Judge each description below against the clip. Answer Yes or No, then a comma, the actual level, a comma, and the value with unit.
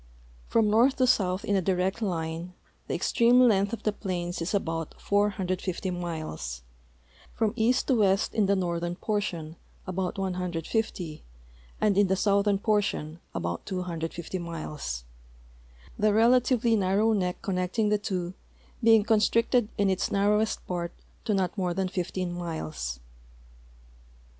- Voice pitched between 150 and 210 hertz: Yes, high, 190 Hz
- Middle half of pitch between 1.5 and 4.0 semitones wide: Yes, average, 3.4 semitones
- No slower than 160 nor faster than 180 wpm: No, slow, 135 wpm